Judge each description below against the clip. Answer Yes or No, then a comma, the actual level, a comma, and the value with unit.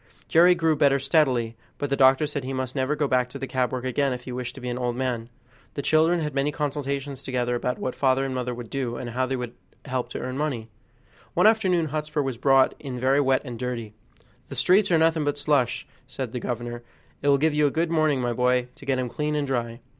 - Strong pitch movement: No, average, 2.9 semitones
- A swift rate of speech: Yes, fast, 245 wpm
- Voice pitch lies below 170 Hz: Yes, low, 135 Hz